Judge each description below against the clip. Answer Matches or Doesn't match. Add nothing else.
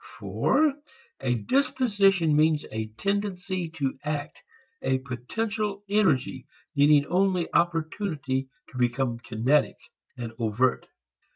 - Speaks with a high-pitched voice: Doesn't match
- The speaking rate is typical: Doesn't match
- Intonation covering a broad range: Matches